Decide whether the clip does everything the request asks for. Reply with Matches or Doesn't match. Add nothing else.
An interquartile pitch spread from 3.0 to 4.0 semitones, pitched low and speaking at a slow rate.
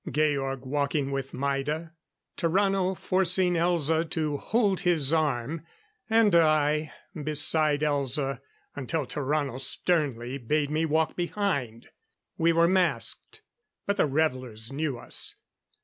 Doesn't match